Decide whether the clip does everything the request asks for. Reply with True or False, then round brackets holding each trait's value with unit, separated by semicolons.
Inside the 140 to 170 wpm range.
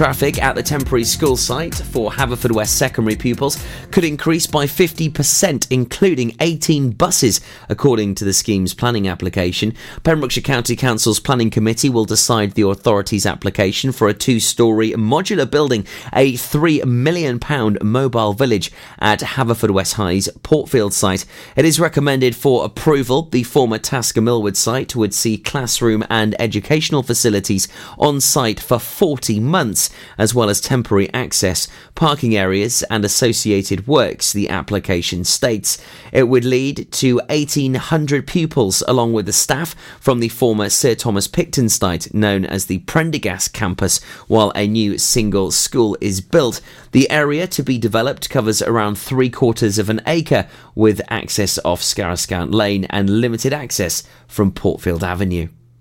True (145 wpm)